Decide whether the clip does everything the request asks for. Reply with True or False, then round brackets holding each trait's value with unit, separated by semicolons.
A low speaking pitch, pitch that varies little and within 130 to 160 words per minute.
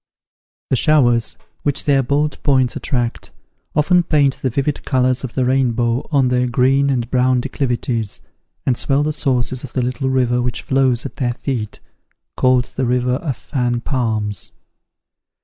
True (130 Hz; 2.1 semitones; 155 wpm)